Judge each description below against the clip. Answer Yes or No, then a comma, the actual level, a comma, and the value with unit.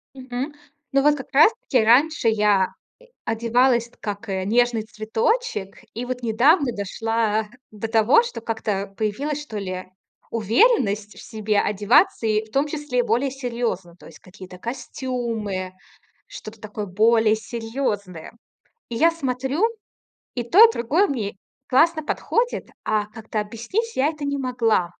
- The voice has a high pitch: Yes, high, 230 Hz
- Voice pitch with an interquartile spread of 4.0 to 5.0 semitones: Yes, average, 4.3 semitones